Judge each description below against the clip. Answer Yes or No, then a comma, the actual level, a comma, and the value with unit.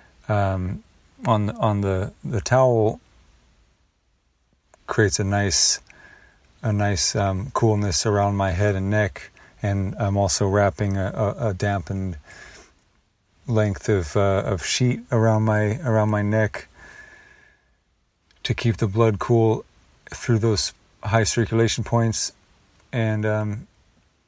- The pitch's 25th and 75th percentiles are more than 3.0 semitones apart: No, narrow, 2.4 semitones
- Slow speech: Yes, slow, 120 wpm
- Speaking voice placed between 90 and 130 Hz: Yes, low, 105 Hz